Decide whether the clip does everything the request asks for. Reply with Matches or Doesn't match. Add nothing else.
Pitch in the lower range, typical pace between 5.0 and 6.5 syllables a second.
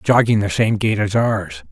Doesn't match